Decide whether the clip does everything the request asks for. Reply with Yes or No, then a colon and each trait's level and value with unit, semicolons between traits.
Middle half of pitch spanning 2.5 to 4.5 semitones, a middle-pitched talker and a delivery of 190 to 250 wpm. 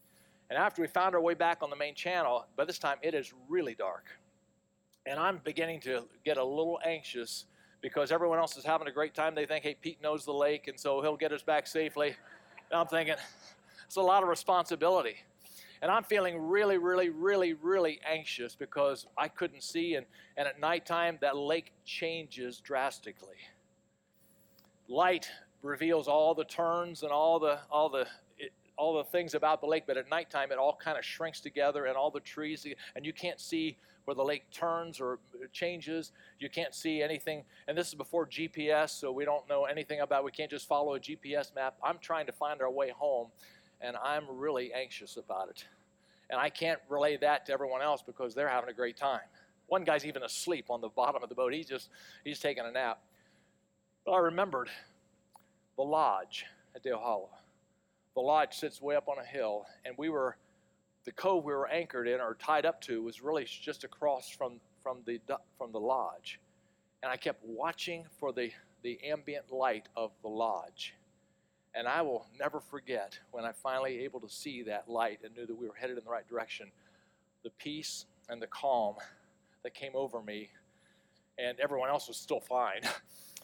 Yes: average, 3.7 semitones; medium, 150 Hz; average, 195 wpm